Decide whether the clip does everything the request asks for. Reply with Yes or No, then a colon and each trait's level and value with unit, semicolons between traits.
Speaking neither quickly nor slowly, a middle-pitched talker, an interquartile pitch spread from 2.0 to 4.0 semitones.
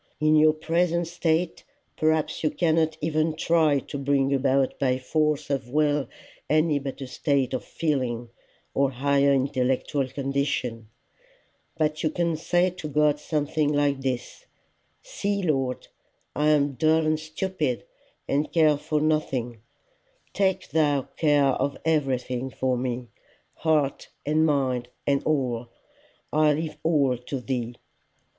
No: slow, 130 wpm; medium, 145 Hz; average, 2.8 semitones